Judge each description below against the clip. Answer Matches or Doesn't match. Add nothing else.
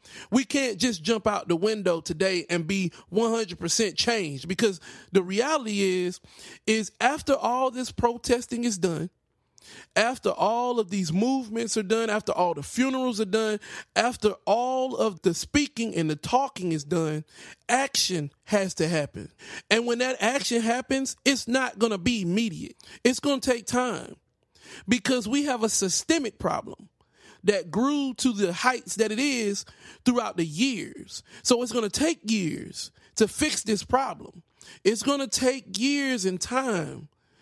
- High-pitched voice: Matches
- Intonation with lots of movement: Doesn't match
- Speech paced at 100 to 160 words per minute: Matches